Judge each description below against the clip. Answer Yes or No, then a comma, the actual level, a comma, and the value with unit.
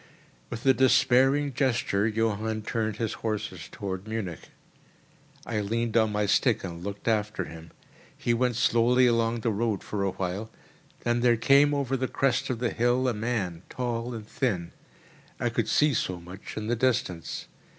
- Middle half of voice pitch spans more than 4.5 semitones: No, average, 3.0 semitones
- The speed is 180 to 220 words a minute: No, average, 170 wpm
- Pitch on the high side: No, low, 115 Hz